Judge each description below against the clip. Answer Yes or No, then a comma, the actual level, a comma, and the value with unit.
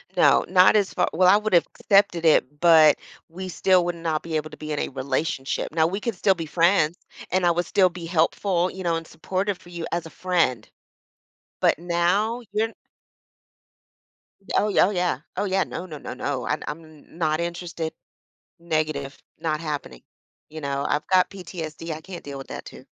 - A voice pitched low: No, medium, 170 Hz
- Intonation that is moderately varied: Yes, average, 3.0 semitones